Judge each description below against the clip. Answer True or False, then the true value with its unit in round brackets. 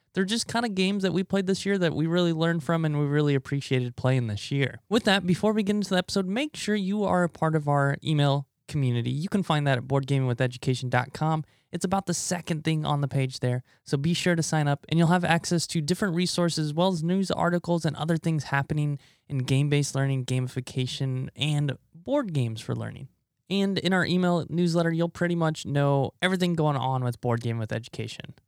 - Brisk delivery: True (220 wpm)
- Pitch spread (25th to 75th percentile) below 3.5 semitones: False (4.7 semitones)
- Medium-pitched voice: True (155 Hz)